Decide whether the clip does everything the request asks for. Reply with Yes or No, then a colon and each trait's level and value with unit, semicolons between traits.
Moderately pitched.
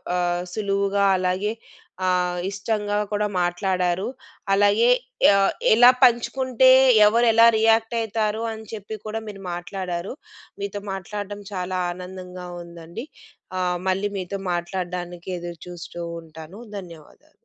No: high, 195 Hz